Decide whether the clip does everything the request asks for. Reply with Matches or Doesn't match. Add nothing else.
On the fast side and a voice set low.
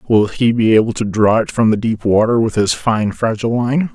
Matches